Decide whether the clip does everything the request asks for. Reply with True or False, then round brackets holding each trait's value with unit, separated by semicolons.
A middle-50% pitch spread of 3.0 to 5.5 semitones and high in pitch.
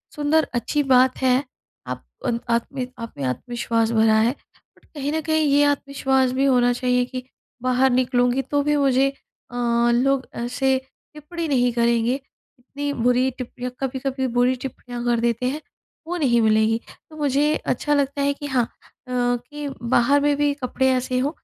False (2.5 semitones; 255 Hz)